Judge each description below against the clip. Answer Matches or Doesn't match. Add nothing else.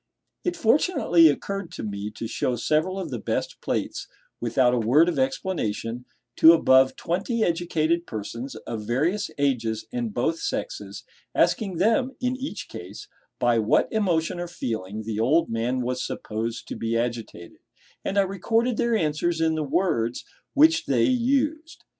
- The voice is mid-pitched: Matches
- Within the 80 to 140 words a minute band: Doesn't match